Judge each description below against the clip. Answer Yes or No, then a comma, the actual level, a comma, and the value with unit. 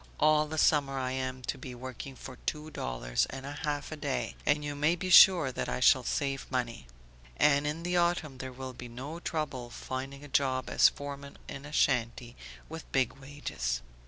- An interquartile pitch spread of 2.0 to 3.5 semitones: Yes, narrow, 2.6 semitones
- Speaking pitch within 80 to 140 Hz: Yes, low, 135 Hz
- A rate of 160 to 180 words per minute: No, average, 195 wpm